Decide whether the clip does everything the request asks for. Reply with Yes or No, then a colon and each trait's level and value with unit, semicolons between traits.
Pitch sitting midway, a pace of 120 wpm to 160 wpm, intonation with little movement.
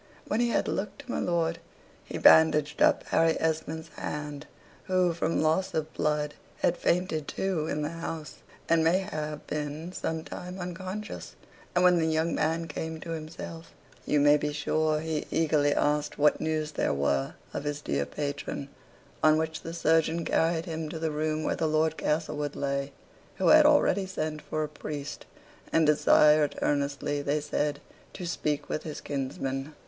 No: medium, 155 Hz; average, 170 wpm; narrow, 1.8 semitones